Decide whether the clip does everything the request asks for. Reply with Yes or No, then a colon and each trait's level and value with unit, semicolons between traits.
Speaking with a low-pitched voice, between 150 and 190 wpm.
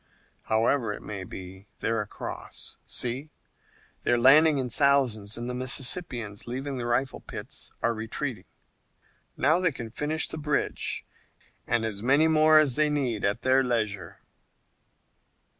No: low, 125 Hz; average, 140 wpm